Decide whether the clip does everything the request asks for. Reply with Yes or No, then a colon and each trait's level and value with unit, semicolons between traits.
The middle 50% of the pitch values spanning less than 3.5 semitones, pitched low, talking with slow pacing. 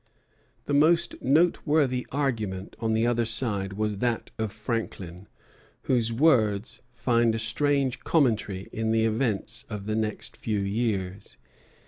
Yes: average, 3.0 semitones; low, 115 Hz; slow, 130 wpm